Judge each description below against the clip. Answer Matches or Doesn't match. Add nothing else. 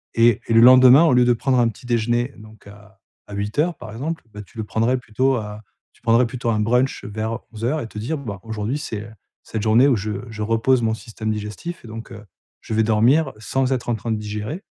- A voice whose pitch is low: Matches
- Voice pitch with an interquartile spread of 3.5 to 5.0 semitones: Doesn't match